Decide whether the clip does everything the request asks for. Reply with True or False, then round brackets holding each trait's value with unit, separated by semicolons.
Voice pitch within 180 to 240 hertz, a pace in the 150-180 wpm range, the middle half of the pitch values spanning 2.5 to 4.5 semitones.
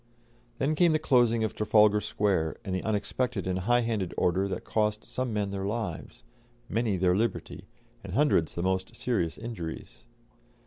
False (105 Hz; 165 wpm; 3.9 semitones)